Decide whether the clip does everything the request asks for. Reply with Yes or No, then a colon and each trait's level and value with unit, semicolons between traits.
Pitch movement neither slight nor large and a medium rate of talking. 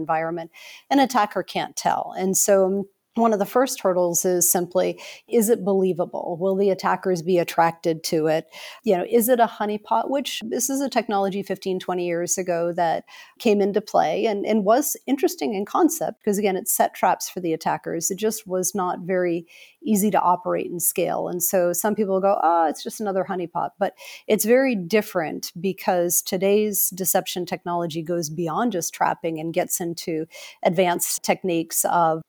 Yes: average, 3.3 semitones; average, 175 wpm